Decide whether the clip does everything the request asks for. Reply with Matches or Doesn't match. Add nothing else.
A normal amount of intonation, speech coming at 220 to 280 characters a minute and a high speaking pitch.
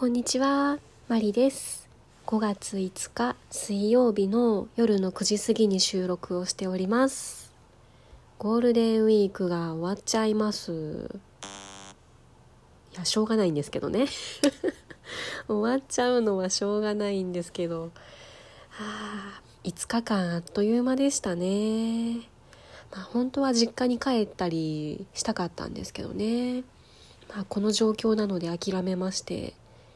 Matches